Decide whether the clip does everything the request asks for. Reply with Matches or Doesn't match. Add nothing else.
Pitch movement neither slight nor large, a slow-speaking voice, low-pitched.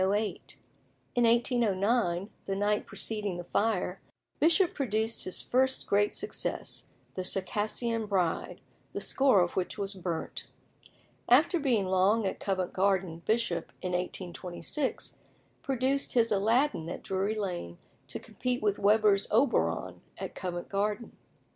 Doesn't match